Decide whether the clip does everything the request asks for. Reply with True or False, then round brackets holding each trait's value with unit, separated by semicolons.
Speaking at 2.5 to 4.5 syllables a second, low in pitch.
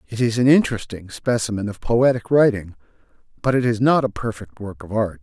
False (5.6 syllables/s; 115 Hz)